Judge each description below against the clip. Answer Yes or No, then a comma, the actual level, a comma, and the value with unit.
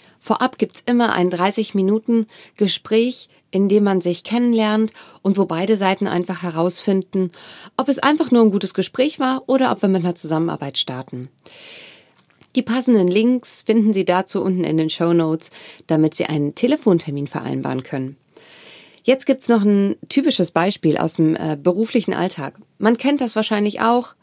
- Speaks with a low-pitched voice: No, high, 195 Hz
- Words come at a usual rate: Yes, average, 160 wpm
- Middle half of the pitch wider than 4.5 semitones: Yes, average, 5.2 semitones